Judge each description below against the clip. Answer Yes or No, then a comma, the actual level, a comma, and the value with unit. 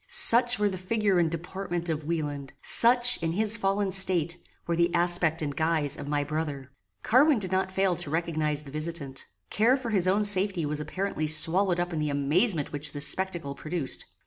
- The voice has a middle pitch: Yes, medium, 170 Hz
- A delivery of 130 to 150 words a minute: No, average, 190 wpm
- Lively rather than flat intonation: No, average, 4.3 semitones